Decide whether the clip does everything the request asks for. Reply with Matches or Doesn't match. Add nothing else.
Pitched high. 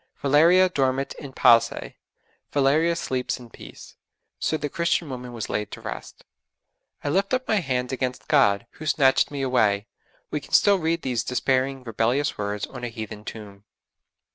Doesn't match